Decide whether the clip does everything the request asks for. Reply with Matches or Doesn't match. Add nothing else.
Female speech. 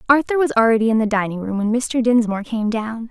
Matches